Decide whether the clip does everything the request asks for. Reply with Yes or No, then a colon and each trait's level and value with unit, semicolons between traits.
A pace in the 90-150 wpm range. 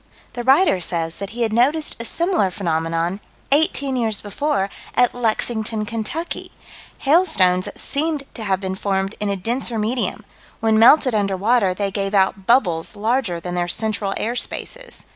No: average, 160 wpm